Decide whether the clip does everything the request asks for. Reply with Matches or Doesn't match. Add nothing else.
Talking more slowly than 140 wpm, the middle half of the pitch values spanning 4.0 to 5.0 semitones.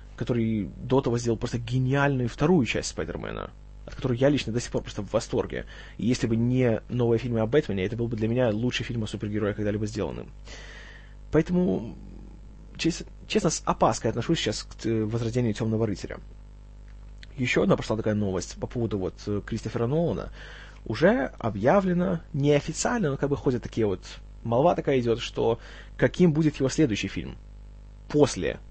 Doesn't match